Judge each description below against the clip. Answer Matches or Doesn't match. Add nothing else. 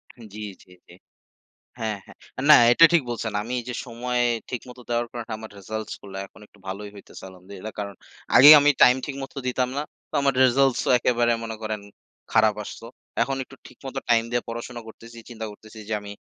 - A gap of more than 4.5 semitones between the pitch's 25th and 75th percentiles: Doesn't match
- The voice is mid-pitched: Doesn't match